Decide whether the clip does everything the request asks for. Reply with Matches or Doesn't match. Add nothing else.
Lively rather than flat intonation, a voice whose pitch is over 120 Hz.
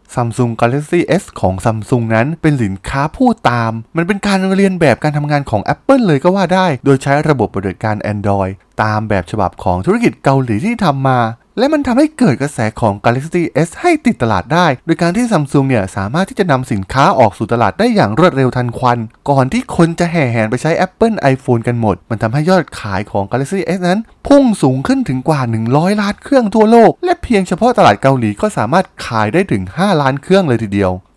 Matches